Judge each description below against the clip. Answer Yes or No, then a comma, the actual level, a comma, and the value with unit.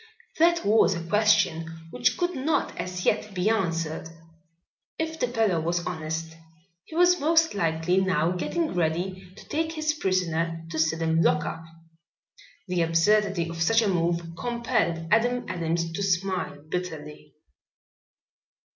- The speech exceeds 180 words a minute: No, average, 140 wpm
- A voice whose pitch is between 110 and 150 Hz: No, medium, 180 Hz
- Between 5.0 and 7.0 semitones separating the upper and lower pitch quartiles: Yes, average, 5.3 semitones